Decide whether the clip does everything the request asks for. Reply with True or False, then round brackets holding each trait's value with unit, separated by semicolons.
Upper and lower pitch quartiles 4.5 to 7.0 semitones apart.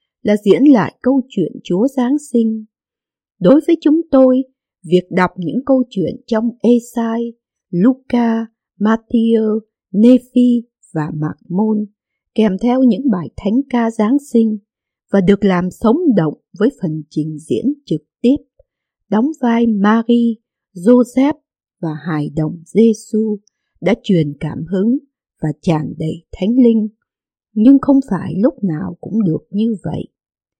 True (5.0 semitones)